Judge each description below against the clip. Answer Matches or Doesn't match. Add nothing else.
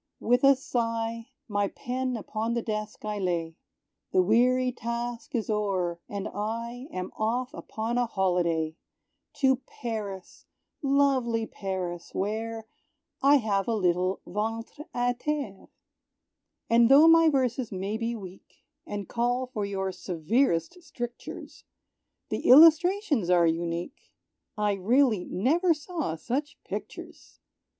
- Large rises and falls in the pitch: Doesn't match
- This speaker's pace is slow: Matches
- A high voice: Matches